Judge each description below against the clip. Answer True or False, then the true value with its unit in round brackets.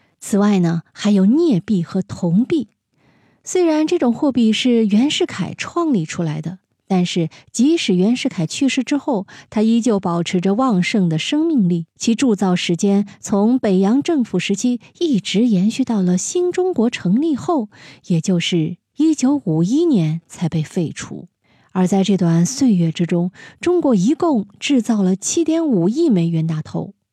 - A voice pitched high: True (210 Hz)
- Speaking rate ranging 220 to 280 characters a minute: True (235 characters per minute)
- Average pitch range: False (7.0 semitones)